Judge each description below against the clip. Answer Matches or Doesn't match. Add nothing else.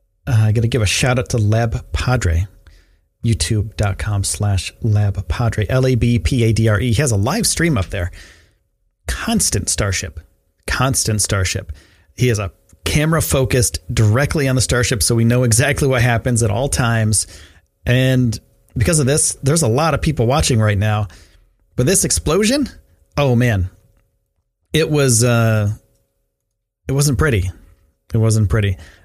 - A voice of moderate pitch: Doesn't match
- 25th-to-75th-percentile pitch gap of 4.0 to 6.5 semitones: Matches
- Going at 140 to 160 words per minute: Matches